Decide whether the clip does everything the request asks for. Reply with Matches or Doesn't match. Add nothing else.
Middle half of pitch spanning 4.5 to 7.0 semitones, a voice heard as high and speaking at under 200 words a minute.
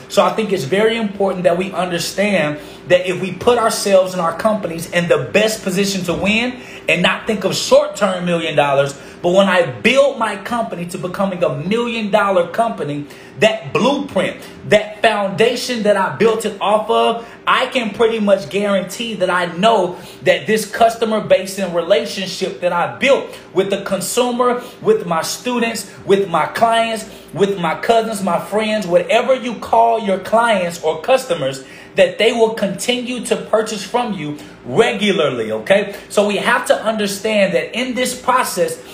Doesn't match